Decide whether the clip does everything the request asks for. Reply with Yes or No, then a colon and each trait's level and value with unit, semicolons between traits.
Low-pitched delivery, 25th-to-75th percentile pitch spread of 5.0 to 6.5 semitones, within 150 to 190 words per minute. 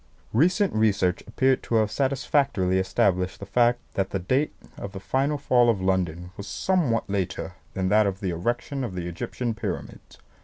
Yes: low, 105 Hz; average, 5.3 semitones; average, 170 wpm